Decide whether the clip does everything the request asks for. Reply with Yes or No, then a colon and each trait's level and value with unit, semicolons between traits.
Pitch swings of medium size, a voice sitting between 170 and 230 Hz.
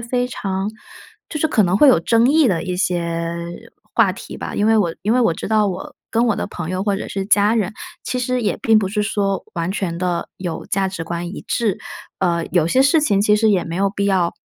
Yes: average, 3.9 semitones; high, 195 Hz